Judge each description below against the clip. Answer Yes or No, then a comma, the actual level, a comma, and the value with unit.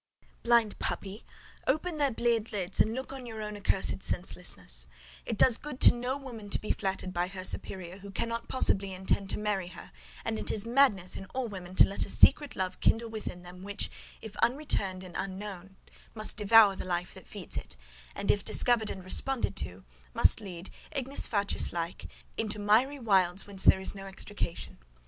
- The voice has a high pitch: Yes, high, 200 Hz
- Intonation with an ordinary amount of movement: Yes, average, 3.8 semitones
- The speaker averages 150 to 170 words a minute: No, average, 185 wpm